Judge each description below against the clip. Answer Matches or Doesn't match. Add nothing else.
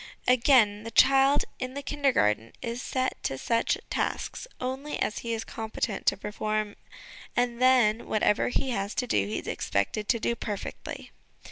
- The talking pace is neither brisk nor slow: Matches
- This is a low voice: Doesn't match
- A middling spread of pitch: Matches